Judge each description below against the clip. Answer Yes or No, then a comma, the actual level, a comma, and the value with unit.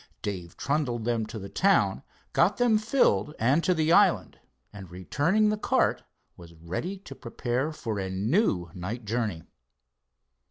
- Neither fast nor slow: Yes, average, 150 wpm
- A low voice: Yes, low, 120 Hz